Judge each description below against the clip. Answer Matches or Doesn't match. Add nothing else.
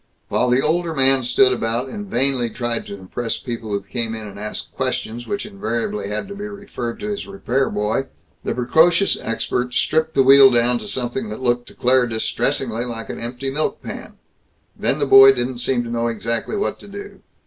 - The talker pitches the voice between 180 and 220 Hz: Doesn't match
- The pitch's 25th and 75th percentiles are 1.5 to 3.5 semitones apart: Matches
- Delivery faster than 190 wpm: Matches